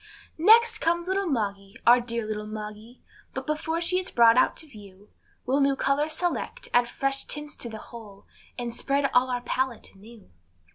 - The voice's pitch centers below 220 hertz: No, very high, 250 Hz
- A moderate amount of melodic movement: No, wide, 5.8 semitones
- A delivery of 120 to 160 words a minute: No, average, 185 wpm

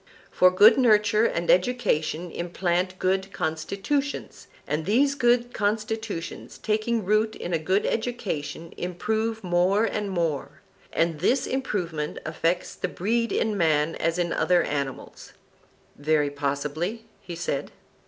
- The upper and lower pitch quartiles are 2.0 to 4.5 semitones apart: No, average, 5.0 semitones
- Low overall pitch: No, medium, 185 Hz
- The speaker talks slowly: Yes, slow, 125 wpm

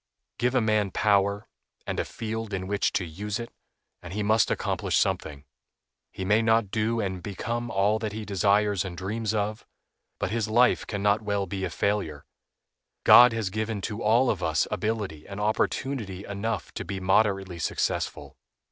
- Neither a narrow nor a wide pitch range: No, narrow, 2.3 semitones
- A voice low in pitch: Yes, low, 105 Hz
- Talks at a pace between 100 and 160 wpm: No, average, 175 wpm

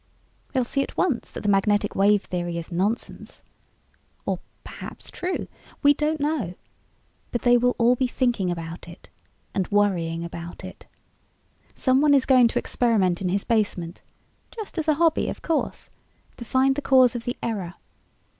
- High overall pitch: Yes, high, 230 Hz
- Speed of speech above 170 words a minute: No, average, 165 wpm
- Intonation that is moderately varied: No, wide, 6.4 semitones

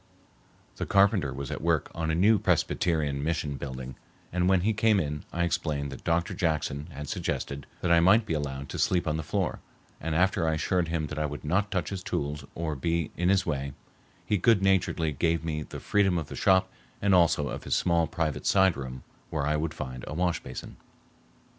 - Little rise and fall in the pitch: No, average, 3.7 semitones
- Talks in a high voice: No, very low, 80 Hz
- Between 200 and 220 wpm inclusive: Yes, fast, 205 wpm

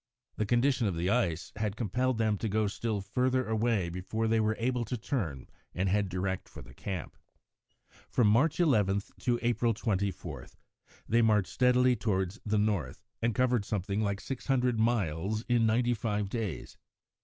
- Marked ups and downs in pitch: No, average, 3.6 semitones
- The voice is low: Yes, low, 110 Hz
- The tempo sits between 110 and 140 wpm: No, average, 165 wpm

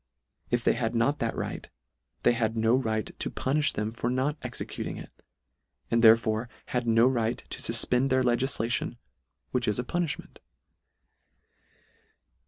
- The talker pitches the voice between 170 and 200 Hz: No, low, 120 Hz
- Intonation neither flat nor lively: No, narrow, 2.2 semitones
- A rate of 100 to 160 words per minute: Yes, average, 155 wpm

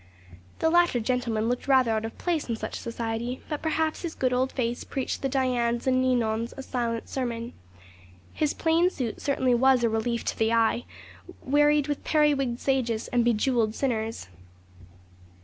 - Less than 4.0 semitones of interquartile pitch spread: Yes, average, 2.9 semitones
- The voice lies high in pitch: Yes, very high, 250 Hz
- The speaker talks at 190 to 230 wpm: No, average, 165 wpm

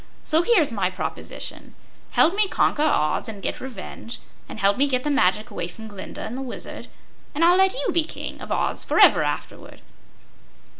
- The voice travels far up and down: Yes, wide, 8.6 semitones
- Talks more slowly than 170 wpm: No, average, 185 wpm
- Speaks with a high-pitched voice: Yes, very high, 260 Hz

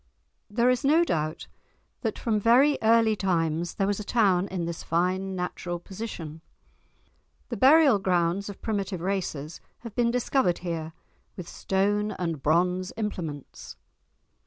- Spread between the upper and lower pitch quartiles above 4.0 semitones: Yes, average, 4.5 semitones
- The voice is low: No, high, 190 Hz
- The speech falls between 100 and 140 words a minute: Yes, slow, 135 wpm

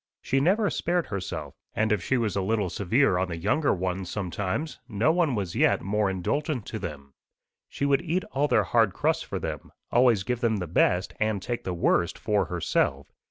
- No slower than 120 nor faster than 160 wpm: No, average, 200 wpm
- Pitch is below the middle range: Yes, low, 105 Hz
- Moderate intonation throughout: No, wide, 6.2 semitones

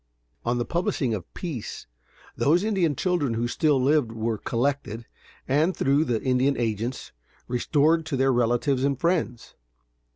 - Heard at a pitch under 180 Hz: Yes, low, 135 Hz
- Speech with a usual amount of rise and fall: Yes, average, 4.4 semitones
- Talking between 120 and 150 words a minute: Yes, average, 140 wpm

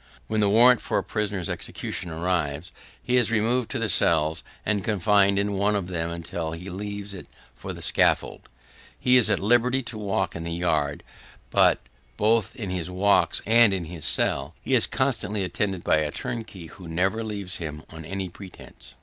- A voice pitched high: No, very low, 95 Hz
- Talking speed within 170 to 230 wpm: Yes, average, 185 wpm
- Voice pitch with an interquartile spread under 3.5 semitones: No, average, 4.1 semitones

